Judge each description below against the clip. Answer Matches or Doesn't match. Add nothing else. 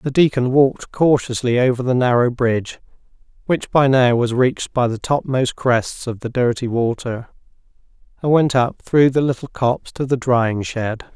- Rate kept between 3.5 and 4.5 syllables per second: Doesn't match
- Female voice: Doesn't match